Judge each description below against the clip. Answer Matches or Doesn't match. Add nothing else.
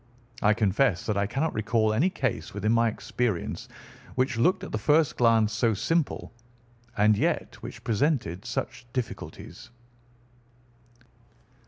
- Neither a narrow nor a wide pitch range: Matches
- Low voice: Matches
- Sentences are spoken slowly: Matches